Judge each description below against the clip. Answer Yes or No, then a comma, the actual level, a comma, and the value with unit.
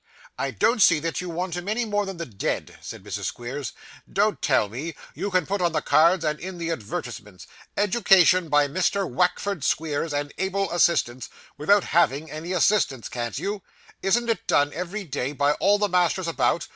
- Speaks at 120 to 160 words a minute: No, average, 185 wpm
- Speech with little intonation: No, average, 5.0 semitones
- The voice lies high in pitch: No, medium, 170 Hz